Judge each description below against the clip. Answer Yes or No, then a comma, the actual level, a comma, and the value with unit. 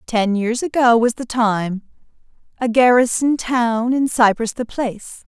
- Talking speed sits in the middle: Yes, average, 145 wpm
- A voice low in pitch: No, high, 235 Hz